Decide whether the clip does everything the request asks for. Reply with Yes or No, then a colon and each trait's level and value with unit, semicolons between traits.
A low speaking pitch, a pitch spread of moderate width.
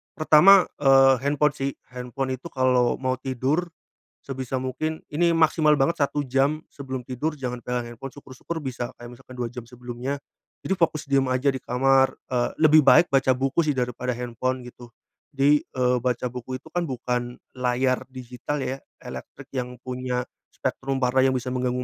No: low, 130 Hz; narrow, 2.0 semitones